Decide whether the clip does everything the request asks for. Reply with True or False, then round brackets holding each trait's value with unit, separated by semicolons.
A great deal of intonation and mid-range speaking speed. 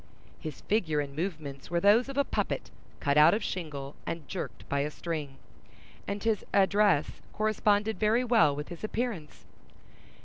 True (6.3 semitones; 160 wpm)